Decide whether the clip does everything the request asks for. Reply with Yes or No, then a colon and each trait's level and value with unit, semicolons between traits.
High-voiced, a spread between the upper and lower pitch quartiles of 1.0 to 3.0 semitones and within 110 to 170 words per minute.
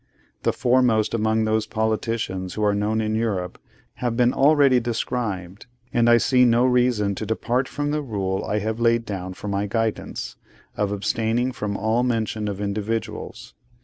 No: low, 110 Hz; average, 2.7 semitones; average, 165 wpm